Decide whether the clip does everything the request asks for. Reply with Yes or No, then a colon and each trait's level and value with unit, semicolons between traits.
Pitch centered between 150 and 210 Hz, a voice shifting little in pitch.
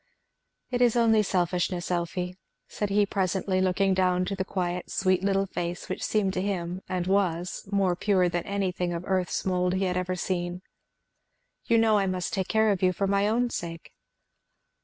Yes: medium, 185 Hz; narrow, 1.8 semitones